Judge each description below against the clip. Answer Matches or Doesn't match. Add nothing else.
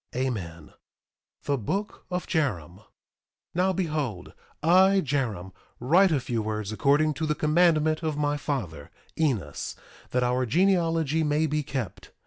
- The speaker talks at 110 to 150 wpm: Matches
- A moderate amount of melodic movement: Doesn't match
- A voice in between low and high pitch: Matches